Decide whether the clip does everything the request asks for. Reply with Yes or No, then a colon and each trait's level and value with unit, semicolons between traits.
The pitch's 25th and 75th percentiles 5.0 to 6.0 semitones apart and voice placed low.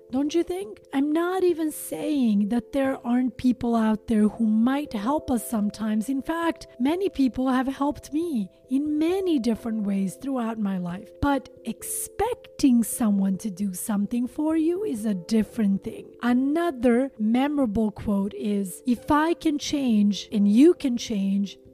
No: wide, 5.4 semitones; high, 245 Hz